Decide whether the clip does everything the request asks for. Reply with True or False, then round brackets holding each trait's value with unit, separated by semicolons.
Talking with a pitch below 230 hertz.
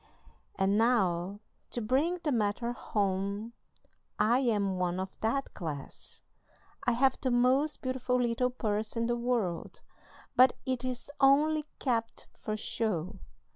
False (235 Hz)